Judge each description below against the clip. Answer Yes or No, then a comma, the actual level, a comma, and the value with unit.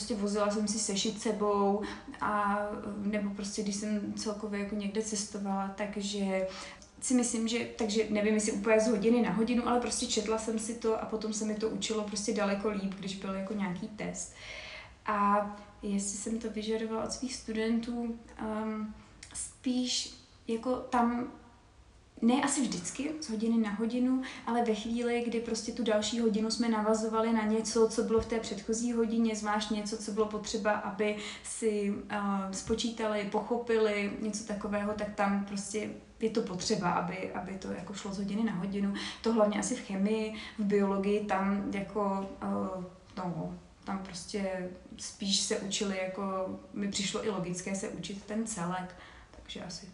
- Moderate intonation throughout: No, narrow, 1.9 semitones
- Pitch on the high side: Yes, high, 215 Hz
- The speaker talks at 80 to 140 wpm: No, average, 165 wpm